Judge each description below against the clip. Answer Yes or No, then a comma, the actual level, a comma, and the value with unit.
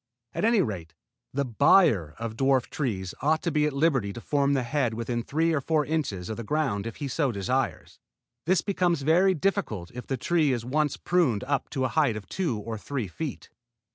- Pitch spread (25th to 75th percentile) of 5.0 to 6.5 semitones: Yes, wide, 5.4 semitones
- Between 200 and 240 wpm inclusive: Yes, fast, 205 wpm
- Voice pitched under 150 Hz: Yes, low, 135 Hz